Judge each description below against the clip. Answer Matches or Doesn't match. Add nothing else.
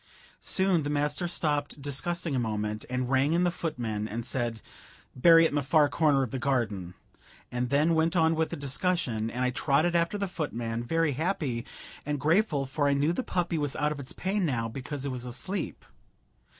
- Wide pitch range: Doesn't match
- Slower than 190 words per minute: Doesn't match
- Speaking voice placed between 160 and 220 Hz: Doesn't match